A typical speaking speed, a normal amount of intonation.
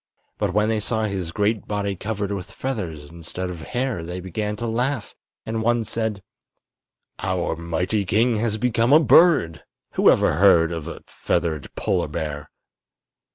Yes: average, 160 wpm; average, 4.8 semitones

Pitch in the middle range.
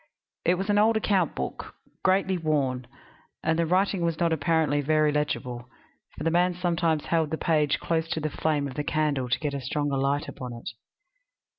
Yes: medium, 155 Hz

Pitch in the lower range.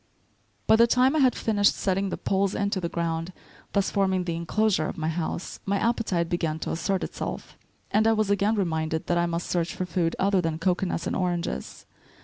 No: medium, 185 Hz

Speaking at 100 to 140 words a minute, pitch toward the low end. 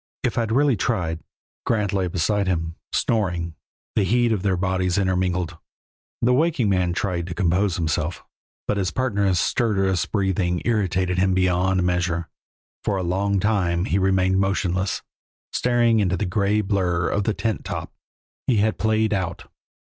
No: average, 155 wpm; very low, 95 Hz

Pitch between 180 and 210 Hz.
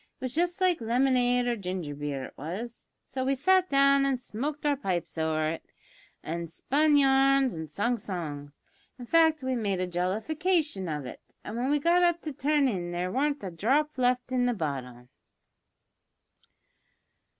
No: high, 245 Hz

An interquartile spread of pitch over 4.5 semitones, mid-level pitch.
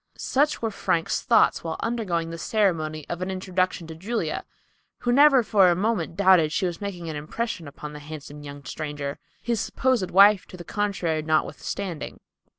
Yes: average, 5.0 semitones; medium, 180 Hz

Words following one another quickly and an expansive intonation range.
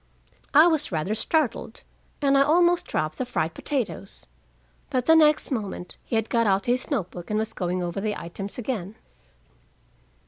No: average, 170 wpm; wide, 6.5 semitones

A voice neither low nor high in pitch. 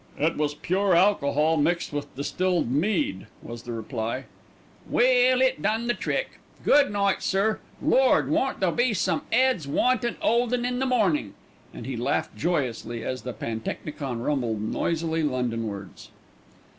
Yes: medium, 165 Hz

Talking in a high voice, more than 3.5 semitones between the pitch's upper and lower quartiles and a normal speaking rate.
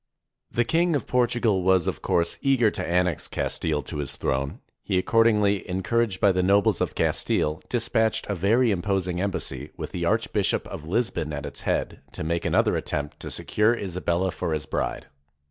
No: very low, 95 Hz; average, 5.1 semitones; average, 180 wpm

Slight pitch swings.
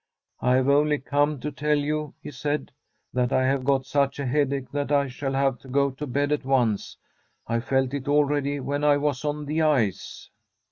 Yes: narrow, 1.9 semitones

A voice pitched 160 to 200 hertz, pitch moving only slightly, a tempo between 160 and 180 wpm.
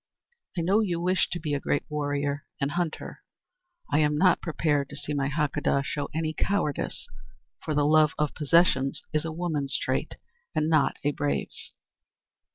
No: medium, 150 Hz; narrow, 2.3 semitones; average, 165 wpm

